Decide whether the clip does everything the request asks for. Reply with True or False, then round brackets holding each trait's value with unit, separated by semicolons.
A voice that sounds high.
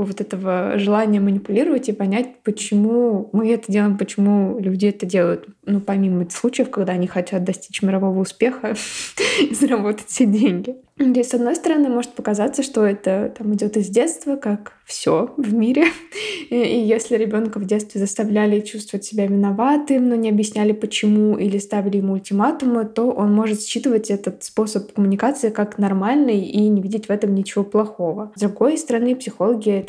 True (215 Hz)